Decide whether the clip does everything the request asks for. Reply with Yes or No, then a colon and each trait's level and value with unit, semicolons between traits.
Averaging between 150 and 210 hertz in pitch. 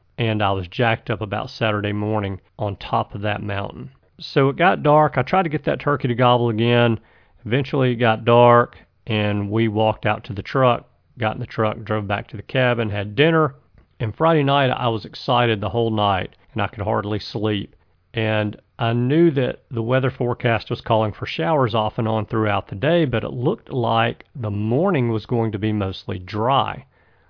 No: low, 115 Hz